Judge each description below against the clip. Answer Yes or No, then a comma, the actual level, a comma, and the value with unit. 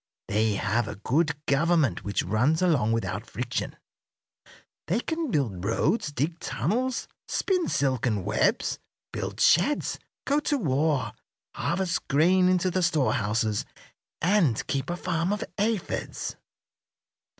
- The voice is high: No, medium, 155 Hz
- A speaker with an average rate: No, slow, 120 wpm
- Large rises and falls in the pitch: Yes, wide, 8.2 semitones